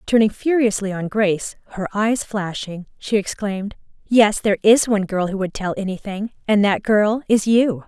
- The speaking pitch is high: Yes, high, 205 Hz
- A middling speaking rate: Yes, average, 175 wpm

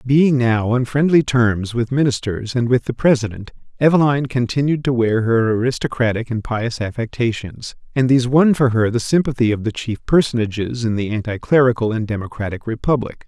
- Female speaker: No, male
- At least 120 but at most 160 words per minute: No, average, 170 wpm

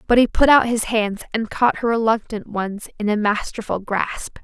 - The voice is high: Yes, high, 220 Hz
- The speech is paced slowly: No, fast, 205 wpm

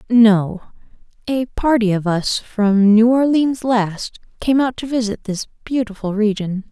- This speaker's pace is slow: No, average, 145 wpm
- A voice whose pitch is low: No, high, 225 Hz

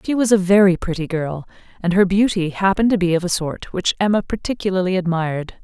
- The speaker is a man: No, female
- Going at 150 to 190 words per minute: No, average, 200 wpm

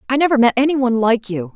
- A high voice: Yes, very high, 250 Hz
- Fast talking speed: Yes, fast, 270 wpm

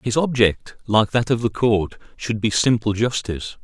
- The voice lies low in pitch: Yes, low, 110 Hz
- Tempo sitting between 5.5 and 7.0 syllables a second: No, 4.6 syllables/s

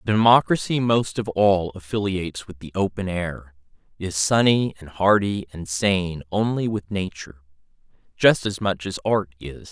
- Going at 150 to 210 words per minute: No, average, 140 wpm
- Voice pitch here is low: Yes, very low, 95 Hz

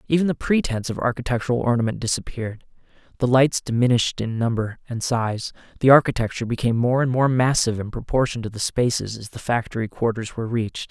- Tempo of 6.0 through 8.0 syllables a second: Yes, 6.5 syllables/s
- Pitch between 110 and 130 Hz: Yes, low, 120 Hz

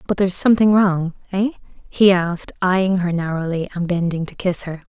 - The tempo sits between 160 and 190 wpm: Yes, average, 170 wpm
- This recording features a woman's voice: Yes, female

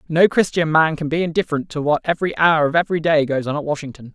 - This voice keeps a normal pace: No, fast, 245 wpm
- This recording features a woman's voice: No, male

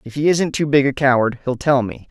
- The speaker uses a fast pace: Yes, fast, 285 wpm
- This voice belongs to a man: Yes, male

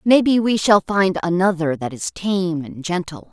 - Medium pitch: Yes, medium, 180 Hz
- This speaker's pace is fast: No, average, 180 wpm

